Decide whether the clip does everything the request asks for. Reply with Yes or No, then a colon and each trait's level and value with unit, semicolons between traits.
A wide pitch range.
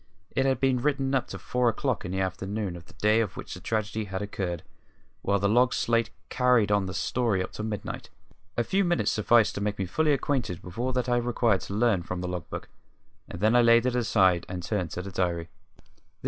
No: average, 4.6 semitones